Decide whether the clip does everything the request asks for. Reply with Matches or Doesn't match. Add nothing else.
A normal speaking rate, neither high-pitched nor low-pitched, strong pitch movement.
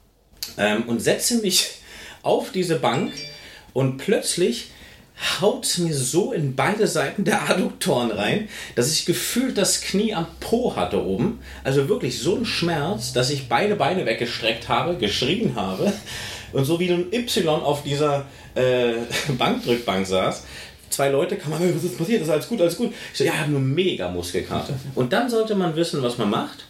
Matches